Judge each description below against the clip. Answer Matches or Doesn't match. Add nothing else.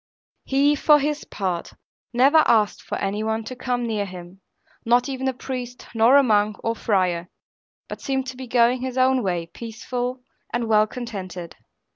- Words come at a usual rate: Matches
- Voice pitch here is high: Matches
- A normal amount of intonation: Matches